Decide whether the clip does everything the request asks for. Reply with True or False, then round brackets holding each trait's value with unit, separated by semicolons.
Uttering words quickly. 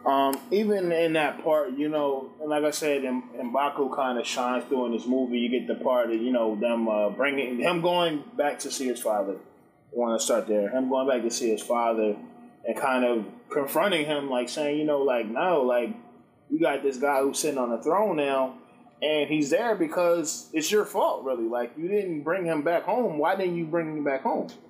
True (225 wpm)